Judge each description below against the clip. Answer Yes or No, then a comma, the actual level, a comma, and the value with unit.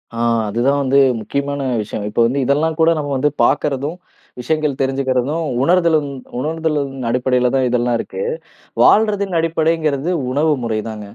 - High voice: No, medium, 140 Hz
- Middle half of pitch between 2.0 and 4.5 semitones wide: Yes, average, 3.9 semitones